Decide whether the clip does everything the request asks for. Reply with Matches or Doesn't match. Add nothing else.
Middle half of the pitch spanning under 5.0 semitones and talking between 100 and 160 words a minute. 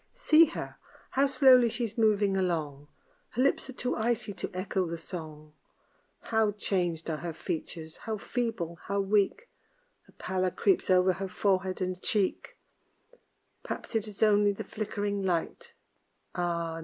Matches